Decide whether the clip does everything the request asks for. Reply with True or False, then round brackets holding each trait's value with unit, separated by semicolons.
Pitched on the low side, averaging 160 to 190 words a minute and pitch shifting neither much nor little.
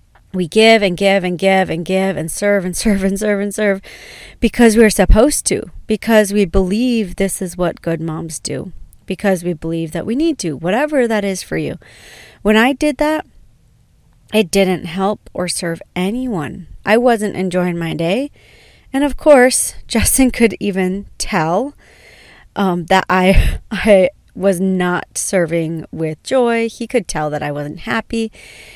False (195 Hz; 165 wpm; 4.0 semitones)